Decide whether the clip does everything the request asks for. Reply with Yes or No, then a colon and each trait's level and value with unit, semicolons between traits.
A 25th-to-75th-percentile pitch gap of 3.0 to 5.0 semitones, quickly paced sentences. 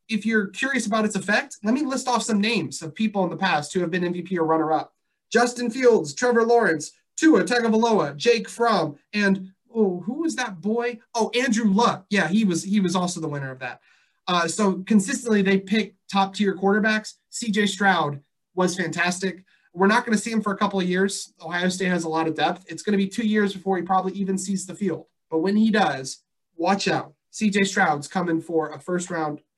Yes: average, 3.8 semitones; fast, 210 wpm